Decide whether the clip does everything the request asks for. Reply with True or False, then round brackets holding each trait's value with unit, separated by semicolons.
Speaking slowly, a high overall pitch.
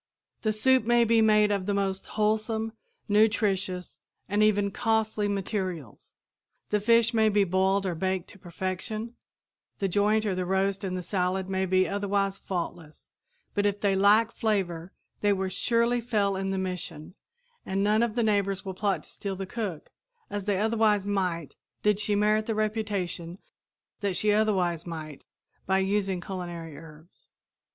False (160 wpm; 200 Hz)